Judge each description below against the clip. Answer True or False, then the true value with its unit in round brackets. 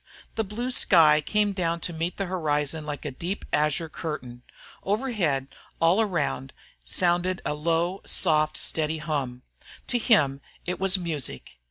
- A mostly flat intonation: False (4.0 semitones)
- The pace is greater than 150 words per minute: False (145 wpm)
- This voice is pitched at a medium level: True (165 Hz)